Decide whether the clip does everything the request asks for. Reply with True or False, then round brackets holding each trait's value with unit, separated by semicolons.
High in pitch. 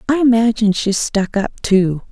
True (215 Hz)